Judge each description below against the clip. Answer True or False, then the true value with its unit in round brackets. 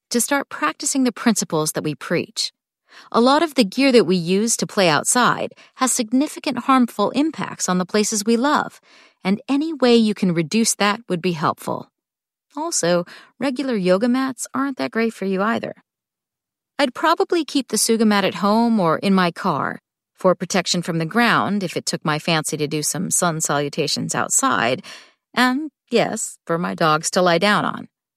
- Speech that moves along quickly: False (180 wpm)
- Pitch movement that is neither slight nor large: False (5.8 semitones)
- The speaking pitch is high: True (210 Hz)